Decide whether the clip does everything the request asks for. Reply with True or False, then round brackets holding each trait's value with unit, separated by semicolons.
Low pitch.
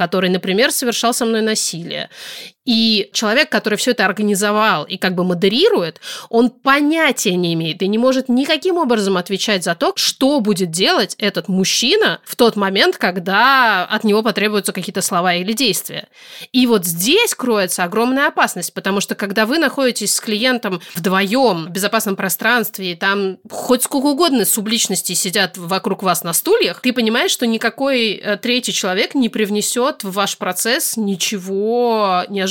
False (215 Hz)